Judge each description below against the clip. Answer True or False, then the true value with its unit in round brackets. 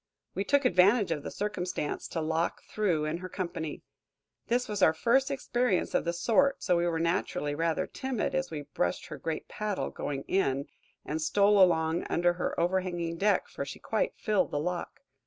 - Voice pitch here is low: False (180 Hz)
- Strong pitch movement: False (4.3 semitones)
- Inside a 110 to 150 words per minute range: False (185 wpm)